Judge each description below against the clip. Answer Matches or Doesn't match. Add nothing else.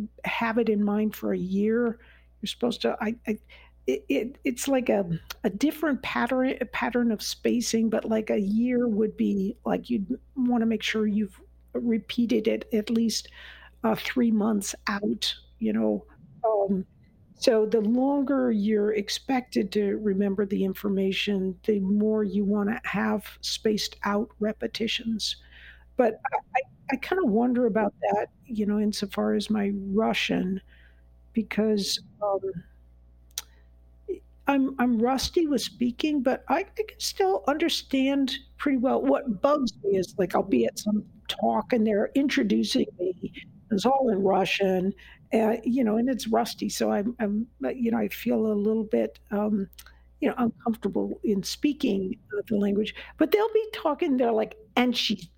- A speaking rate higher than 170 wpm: Doesn't match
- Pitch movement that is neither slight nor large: Matches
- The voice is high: Matches